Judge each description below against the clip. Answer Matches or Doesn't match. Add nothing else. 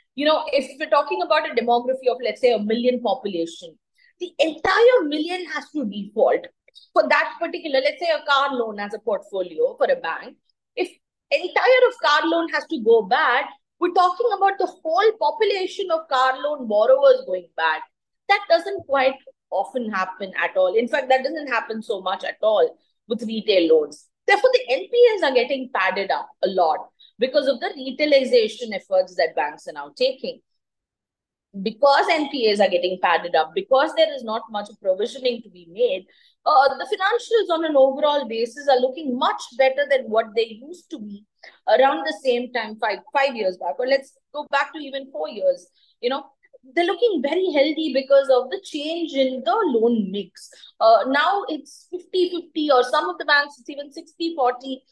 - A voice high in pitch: Matches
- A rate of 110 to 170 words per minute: Doesn't match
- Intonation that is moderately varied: Doesn't match